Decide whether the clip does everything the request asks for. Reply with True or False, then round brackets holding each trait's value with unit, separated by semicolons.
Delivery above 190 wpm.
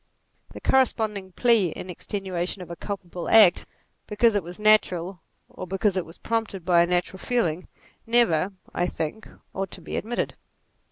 False (160 wpm)